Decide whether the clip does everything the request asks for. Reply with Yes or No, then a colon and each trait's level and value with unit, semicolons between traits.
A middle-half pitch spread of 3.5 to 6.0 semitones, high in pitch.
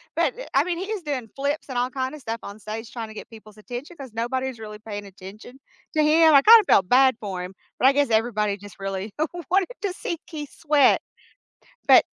Yes: wide, 5.5 semitones; high, 245 Hz